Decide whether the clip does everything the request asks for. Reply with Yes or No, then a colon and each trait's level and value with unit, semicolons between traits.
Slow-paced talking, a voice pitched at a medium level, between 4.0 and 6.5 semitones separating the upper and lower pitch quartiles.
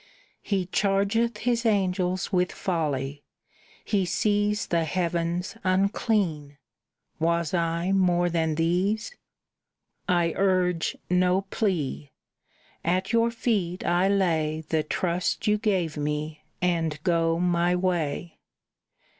No: slow, 105 wpm; medium, 180 Hz; average, 2.9 semitones